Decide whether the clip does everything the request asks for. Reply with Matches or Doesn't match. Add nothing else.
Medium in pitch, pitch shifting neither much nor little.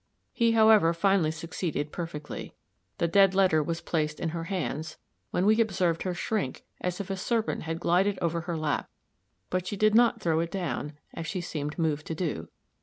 Matches